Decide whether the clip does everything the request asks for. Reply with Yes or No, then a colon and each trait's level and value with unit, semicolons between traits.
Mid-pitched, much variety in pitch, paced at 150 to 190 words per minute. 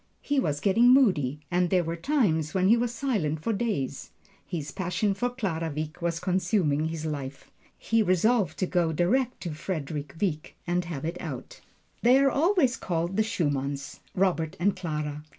Yes: medium, 175 Hz; wide, 6.0 semitones; average, 170 wpm